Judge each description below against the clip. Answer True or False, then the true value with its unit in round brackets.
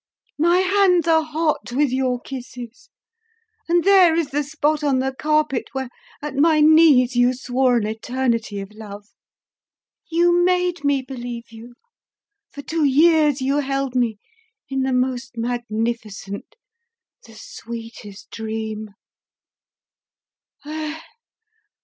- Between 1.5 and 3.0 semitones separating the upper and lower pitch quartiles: False (4.6 semitones)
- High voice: True (265 Hz)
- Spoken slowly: True (120 wpm)